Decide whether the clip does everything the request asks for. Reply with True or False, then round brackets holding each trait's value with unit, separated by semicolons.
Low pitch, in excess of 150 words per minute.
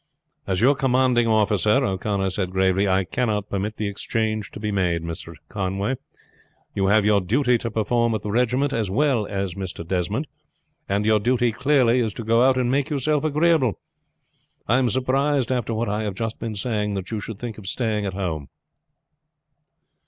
True (110 Hz; 180 wpm)